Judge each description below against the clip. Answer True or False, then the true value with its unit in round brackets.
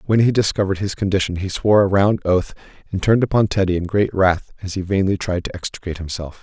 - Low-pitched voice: True (95 Hz)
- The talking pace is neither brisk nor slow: False (225 wpm)